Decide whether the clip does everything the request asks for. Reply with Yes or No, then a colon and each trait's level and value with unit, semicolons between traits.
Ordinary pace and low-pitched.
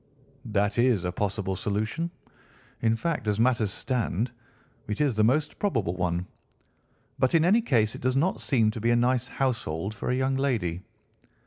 Yes: average, 165 wpm; low, 115 Hz